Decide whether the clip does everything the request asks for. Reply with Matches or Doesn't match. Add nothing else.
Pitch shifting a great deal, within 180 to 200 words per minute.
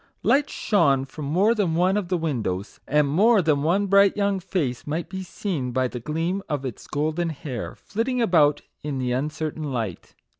Matches